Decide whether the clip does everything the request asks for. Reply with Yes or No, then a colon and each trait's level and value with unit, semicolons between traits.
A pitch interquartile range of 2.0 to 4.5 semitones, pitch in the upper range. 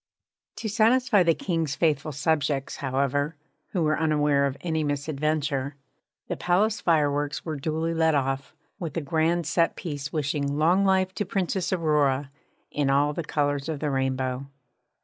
No: average, 2.9 semitones; medium, 150 Hz